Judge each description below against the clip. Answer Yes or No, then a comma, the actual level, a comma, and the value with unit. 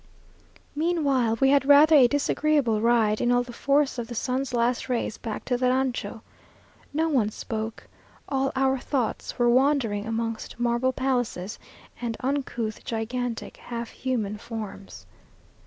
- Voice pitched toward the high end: Yes, high, 245 Hz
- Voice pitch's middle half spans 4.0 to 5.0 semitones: No, average, 2.9 semitones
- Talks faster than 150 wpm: No, average, 140 wpm